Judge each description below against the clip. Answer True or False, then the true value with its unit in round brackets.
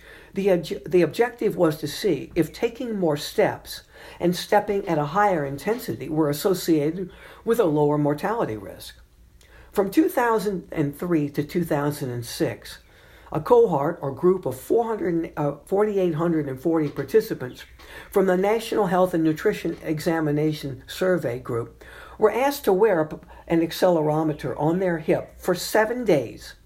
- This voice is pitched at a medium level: True (170 Hz)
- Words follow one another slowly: True (125 wpm)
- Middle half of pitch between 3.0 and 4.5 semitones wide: False (5.0 semitones)